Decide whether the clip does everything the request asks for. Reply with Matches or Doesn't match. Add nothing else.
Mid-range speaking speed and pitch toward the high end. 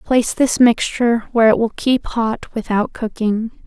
Matches